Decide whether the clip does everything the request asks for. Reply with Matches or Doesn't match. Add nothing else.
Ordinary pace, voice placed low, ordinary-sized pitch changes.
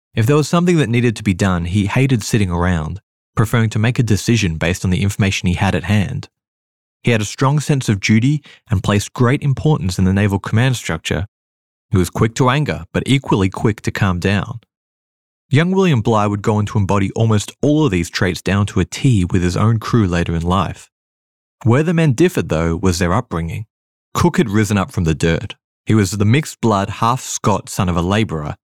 Doesn't match